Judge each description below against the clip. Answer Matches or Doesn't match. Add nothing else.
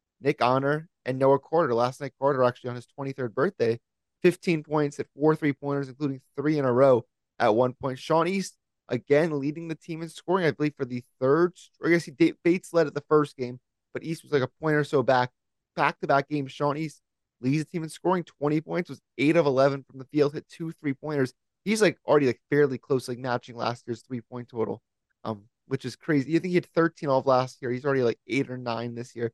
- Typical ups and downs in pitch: Matches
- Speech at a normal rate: Doesn't match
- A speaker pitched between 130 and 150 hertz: Matches